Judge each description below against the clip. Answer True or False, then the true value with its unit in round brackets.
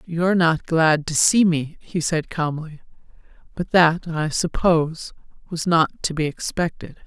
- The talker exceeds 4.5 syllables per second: False (4.4 syllables/s)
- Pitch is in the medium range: True (165 Hz)